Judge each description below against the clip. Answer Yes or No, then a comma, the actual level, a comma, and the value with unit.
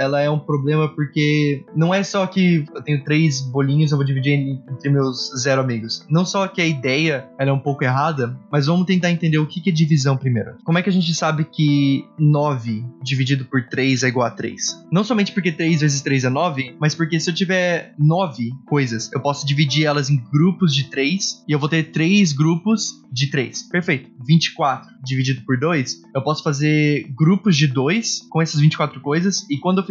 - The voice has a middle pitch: Yes, medium, 150 Hz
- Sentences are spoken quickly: Yes, fast, 210 wpm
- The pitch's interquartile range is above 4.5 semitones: No, average, 3.5 semitones